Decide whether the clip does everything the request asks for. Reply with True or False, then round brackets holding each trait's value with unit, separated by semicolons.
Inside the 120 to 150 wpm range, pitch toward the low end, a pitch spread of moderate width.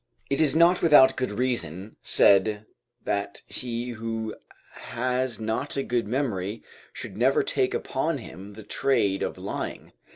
True (140 wpm; 115 Hz; 4.0 semitones)